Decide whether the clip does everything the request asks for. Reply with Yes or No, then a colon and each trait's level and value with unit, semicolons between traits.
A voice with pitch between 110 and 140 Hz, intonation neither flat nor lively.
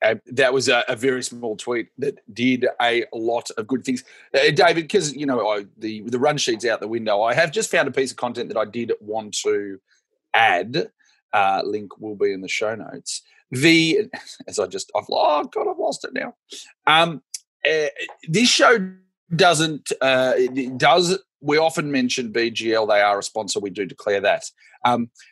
No: low, 135 Hz; wide, 8.0 semitones